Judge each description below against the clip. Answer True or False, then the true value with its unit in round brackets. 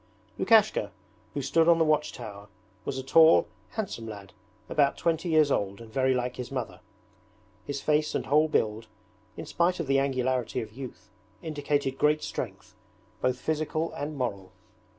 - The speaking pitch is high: False (140 Hz)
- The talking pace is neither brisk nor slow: True (160 wpm)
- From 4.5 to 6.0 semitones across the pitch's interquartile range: False (4.1 semitones)